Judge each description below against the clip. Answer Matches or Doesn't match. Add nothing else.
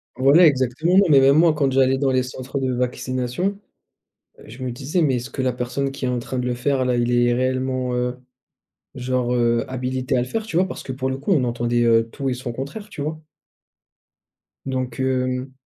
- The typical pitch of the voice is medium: Doesn't match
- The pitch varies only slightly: Matches